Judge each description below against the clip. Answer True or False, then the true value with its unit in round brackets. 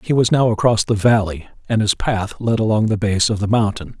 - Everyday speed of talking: False (240 wpm)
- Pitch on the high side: False (105 Hz)